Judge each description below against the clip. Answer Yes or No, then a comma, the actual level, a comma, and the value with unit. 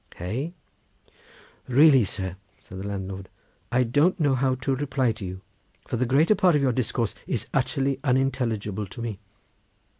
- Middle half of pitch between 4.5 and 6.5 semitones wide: Yes, average, 5.1 semitones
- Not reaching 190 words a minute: Yes, average, 155 wpm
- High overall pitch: No, low, 125 Hz